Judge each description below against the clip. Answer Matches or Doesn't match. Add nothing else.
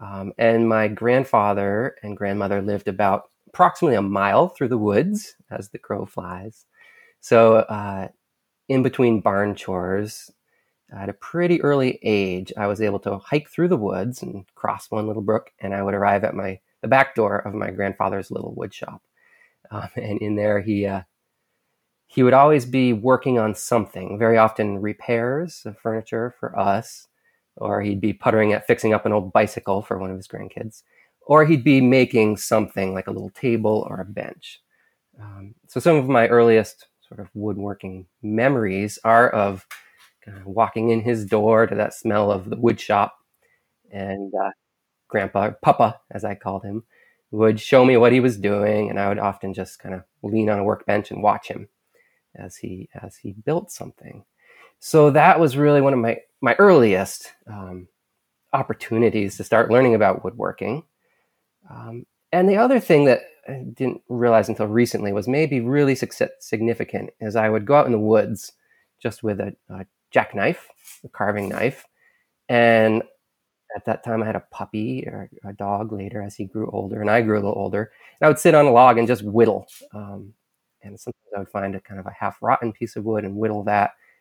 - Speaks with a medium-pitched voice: Doesn't match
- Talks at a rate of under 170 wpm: Doesn't match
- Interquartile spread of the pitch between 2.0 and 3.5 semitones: Matches